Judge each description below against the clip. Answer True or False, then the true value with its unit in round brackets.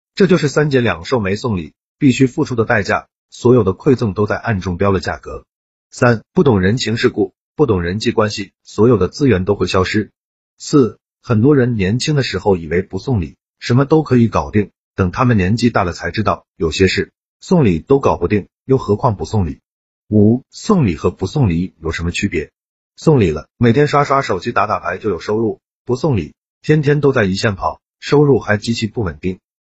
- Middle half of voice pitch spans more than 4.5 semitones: True (5.5 semitones)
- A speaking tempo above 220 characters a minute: True (290 characters per minute)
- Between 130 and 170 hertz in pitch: False (110 Hz)